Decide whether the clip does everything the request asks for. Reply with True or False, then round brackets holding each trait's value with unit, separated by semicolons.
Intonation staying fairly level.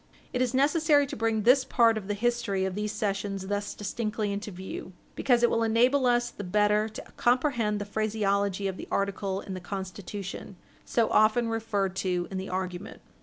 False (3.1 semitones)